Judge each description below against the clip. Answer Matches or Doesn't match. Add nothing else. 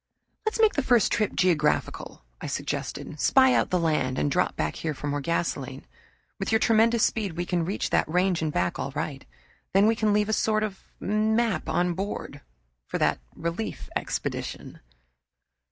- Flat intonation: Doesn't match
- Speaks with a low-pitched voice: Doesn't match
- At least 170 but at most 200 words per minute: Matches